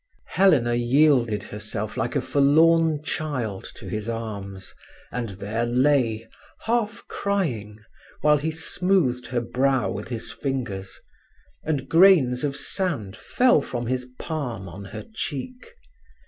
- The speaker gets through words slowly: Yes, slow, 125 wpm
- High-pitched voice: No, low, 130 Hz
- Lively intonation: Yes, wide, 5.8 semitones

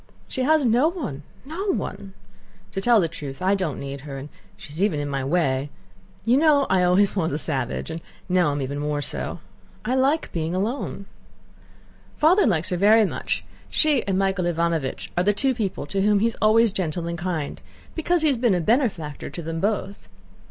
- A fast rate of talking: No, average, 195 wpm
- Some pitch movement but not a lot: No, wide, 6.7 semitones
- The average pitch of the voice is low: No, high, 190 Hz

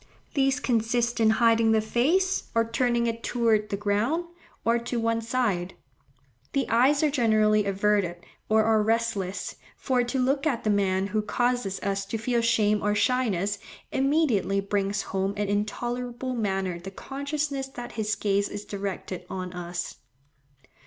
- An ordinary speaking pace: Yes, average, 155 wpm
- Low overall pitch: No, high, 225 Hz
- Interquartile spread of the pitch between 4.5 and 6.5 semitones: No, average, 3.4 semitones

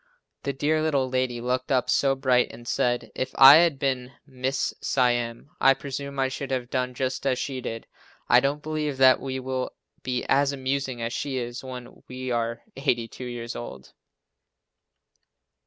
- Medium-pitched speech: No, low, 130 Hz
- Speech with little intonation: Yes, narrow, 1.8 semitones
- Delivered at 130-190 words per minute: Yes, average, 170 wpm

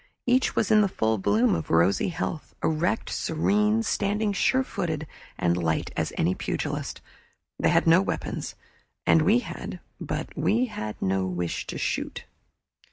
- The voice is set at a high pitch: No, medium, 160 Hz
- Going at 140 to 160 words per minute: Yes, average, 155 wpm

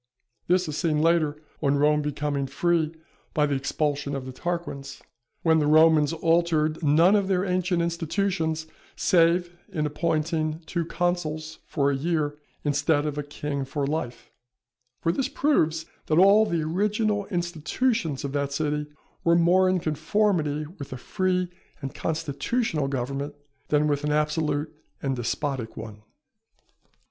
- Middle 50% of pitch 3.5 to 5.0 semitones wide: No, average, 2.9 semitones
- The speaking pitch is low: No, medium, 155 Hz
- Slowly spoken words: No, average, 145 wpm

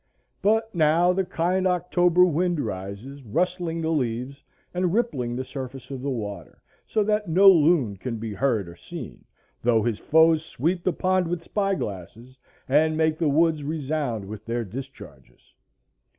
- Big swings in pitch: Yes, wide, 6.6 semitones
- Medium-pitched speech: Yes, medium, 155 Hz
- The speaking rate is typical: Yes, average, 160 wpm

